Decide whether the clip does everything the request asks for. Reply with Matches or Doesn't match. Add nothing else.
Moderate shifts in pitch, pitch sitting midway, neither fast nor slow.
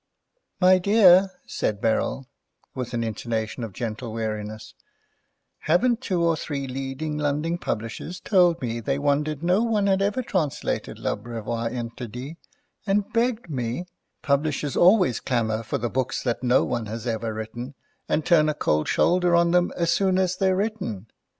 Doesn't match